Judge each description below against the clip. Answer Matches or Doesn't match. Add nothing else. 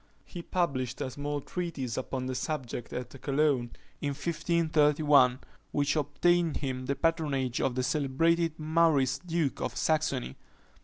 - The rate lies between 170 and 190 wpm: Doesn't match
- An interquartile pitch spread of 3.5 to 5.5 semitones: Matches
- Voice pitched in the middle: Matches